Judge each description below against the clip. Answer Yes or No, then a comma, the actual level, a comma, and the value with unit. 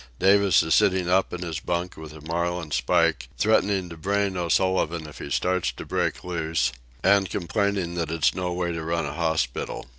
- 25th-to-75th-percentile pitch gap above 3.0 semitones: No, narrow, 2.5 semitones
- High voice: No, very low, 85 Hz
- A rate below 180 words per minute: No, average, 185 wpm